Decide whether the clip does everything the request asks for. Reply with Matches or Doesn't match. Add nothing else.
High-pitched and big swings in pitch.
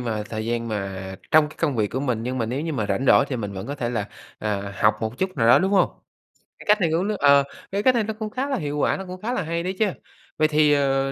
Doesn't match